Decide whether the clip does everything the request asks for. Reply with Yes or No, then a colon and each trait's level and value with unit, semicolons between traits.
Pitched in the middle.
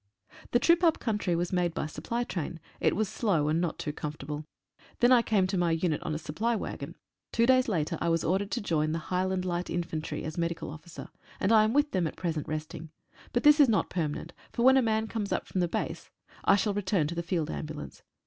Yes: medium, 180 Hz